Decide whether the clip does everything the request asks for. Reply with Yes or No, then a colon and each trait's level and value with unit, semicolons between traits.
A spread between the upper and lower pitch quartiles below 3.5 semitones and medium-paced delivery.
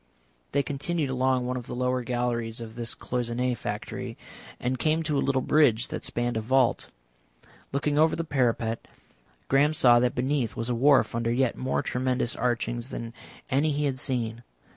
Yes: narrow, 2.6 semitones; average, 175 wpm